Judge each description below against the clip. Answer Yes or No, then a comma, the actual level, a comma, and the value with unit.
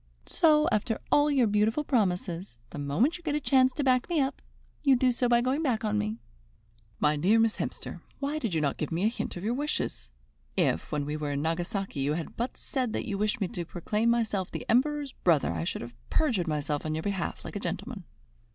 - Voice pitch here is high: Yes, high, 215 Hz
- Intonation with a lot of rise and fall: Yes, wide, 7.7 semitones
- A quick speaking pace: Yes, fast, 225 wpm